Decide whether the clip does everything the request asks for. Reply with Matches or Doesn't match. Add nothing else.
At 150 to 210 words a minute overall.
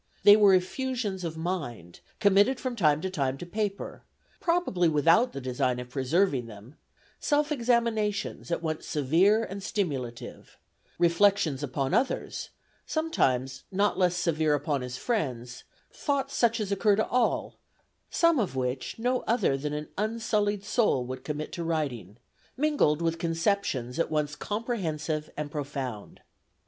Doesn't match